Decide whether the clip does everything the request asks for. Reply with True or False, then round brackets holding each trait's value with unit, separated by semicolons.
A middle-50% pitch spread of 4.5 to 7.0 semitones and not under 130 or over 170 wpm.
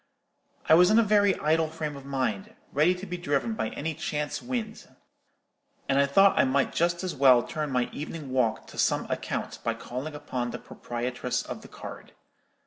False (5.2 semitones; 190 wpm)